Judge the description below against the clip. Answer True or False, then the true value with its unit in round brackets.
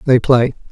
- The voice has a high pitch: False (130 Hz)